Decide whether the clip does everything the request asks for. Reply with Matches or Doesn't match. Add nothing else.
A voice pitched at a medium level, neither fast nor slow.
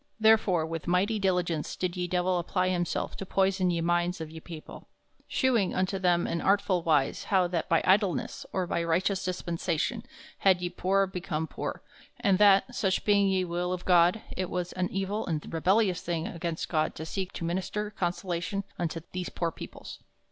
Matches